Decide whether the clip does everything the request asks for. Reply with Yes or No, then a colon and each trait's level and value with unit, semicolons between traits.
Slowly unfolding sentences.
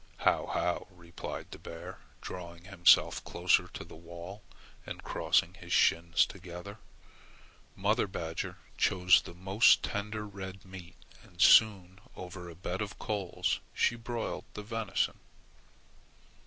Yes: slow, 130 wpm